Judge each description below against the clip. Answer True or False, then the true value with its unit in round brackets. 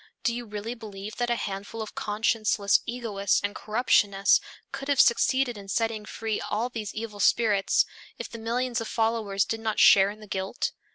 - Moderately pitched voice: False (220 Hz)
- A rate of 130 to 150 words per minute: False (180 wpm)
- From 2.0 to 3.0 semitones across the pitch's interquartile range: True (2.4 semitones)